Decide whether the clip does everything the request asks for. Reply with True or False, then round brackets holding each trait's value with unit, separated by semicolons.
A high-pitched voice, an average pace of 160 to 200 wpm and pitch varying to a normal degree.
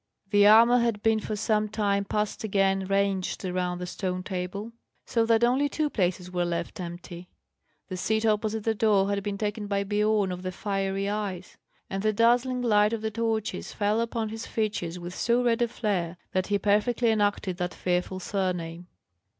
True (205 Hz; 185 wpm; 3.0 semitones)